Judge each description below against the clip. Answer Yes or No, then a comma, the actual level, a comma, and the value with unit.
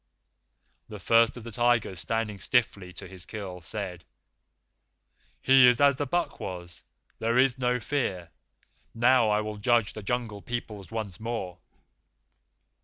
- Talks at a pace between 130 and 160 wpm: Yes, average, 140 wpm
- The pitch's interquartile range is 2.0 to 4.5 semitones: Yes, average, 3.8 semitones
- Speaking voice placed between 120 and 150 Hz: No, low, 110 Hz